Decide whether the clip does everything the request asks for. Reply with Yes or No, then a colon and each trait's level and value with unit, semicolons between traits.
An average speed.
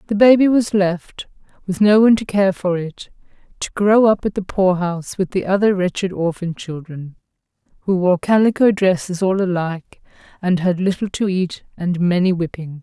Yes: average, 175 wpm